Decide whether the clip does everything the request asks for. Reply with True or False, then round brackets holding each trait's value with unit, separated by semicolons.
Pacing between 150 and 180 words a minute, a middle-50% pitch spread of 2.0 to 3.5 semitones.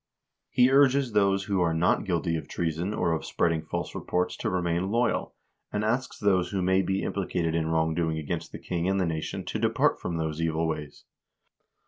False (195 wpm; 3.2 semitones)